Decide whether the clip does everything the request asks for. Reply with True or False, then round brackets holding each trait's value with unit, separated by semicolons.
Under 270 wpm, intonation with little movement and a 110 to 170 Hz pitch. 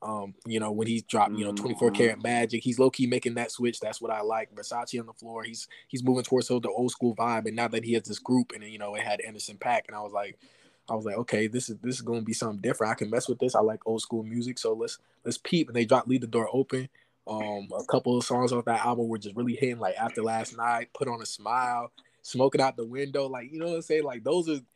False (285 wpm; 2.1 semitones; 120 Hz)